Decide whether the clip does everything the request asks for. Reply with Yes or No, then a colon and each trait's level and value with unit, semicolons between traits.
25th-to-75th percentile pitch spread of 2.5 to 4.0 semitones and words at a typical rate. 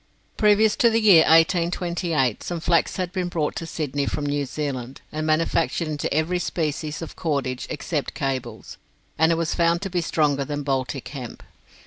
Yes: average, 3.3 semitones; average, 170 wpm